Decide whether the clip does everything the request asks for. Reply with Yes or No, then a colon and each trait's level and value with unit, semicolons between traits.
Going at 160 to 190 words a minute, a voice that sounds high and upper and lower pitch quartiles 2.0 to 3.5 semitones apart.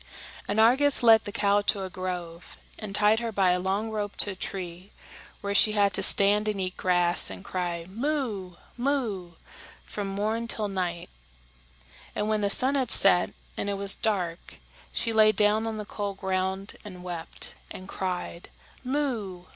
Yes: average, 170 wpm; high, 200 Hz; average, 2.8 semitones